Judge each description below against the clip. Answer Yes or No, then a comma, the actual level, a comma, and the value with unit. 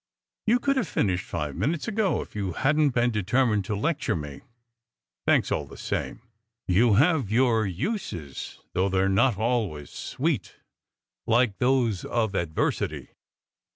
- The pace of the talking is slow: No, average, 150 wpm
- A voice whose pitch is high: No, low, 115 Hz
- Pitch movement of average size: No, wide, 5.9 semitones